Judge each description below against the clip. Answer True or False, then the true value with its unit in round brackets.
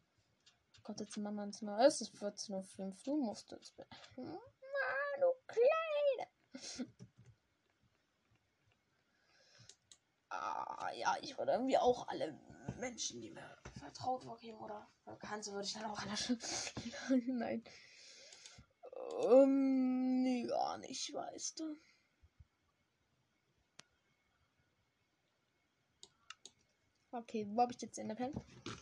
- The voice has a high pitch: True (255 Hz)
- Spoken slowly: True (105 wpm)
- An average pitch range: True (4.6 semitones)